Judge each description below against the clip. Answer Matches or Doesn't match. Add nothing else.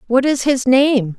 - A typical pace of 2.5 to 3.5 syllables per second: Doesn't match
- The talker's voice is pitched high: Matches